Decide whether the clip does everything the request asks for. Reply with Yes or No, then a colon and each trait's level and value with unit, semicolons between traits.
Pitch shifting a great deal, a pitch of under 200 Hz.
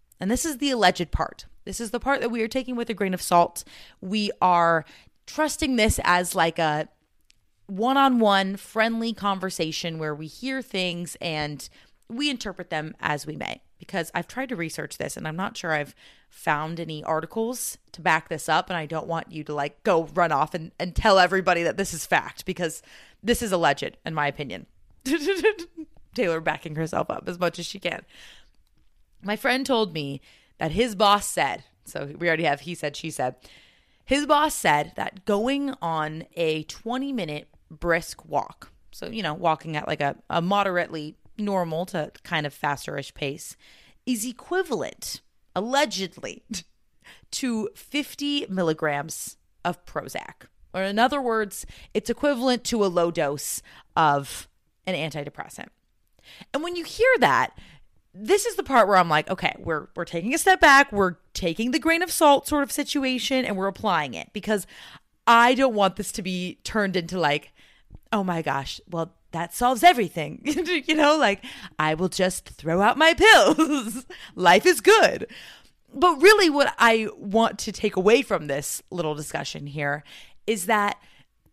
Yes: wide, 7.3 semitones; high, 190 Hz